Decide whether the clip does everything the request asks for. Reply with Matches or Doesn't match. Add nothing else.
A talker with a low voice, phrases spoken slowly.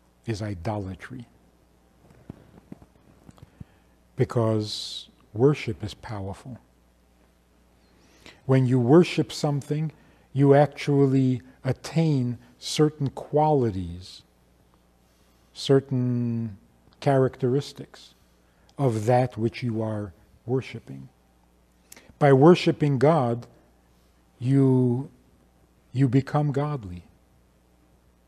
Matches